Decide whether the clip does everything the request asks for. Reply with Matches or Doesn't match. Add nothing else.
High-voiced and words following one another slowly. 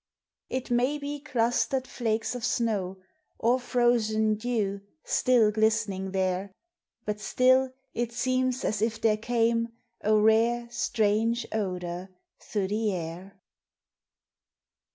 Matches